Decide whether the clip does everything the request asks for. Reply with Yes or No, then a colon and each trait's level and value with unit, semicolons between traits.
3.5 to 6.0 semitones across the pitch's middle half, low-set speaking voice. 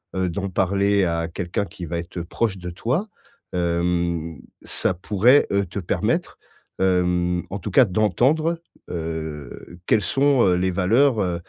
No: average, 3.0 semitones; very low, 90 Hz